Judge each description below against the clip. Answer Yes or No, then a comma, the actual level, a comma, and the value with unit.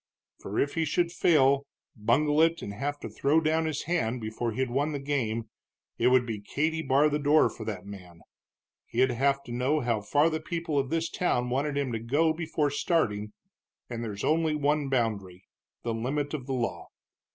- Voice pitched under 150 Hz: Yes, medium, 140 Hz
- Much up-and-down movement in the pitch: No, average, 4.8 semitones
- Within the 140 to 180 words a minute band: No, average, 195 wpm